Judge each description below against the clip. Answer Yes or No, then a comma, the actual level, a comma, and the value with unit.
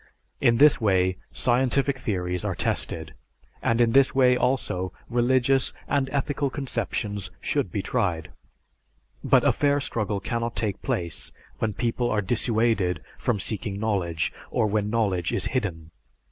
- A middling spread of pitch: Yes, average, 4.7 semitones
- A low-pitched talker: Yes, low, 115 Hz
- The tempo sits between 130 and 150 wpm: Yes, average, 145 wpm